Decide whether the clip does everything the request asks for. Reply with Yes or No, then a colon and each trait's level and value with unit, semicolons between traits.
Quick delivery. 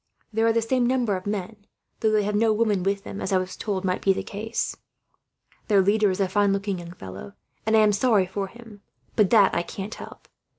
Yes: fast, 230 wpm